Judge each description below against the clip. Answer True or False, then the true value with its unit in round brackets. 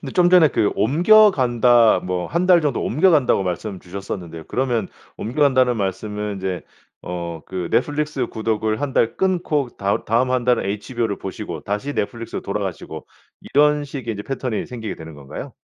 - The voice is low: True (115 Hz)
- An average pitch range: False (6.2 semitones)